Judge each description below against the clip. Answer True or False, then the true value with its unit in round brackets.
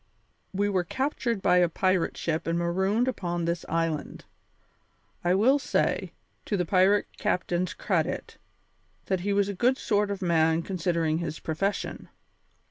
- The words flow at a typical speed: True (145 wpm)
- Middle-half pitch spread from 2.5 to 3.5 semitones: True (3.1 semitones)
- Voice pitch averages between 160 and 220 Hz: True (185 Hz)